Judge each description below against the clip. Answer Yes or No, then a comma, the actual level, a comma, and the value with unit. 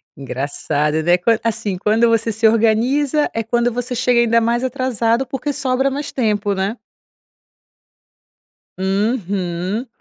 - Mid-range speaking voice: No, high, 230 Hz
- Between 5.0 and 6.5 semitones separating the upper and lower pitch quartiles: No, average, 4.0 semitones